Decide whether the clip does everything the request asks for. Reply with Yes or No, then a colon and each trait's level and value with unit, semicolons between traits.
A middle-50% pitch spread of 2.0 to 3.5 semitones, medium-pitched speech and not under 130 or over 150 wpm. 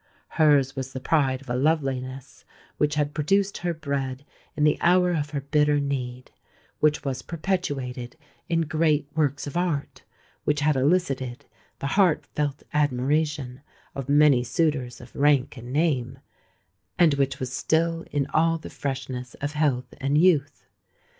Yes: average, 2.9 semitones; medium, 145 Hz; average, 140 wpm